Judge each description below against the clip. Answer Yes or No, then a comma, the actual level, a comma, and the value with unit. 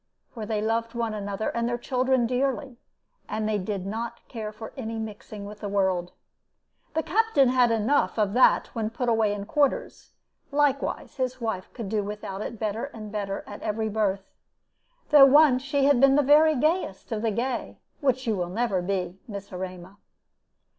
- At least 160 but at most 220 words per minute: Yes, average, 180 wpm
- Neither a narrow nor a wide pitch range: Yes, average, 4.0 semitones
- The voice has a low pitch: No, high, 225 Hz